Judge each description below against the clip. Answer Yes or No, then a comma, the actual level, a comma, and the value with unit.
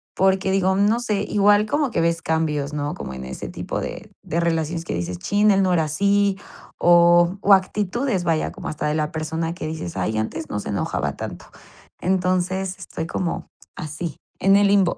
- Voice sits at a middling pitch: Yes, medium, 175 Hz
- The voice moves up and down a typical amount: Yes, average, 3.8 semitones